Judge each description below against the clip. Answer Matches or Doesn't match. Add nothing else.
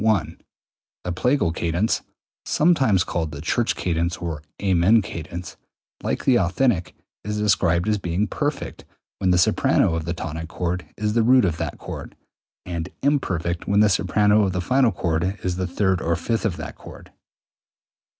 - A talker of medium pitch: Doesn't match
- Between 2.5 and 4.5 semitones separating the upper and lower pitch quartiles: Matches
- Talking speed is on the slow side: Doesn't match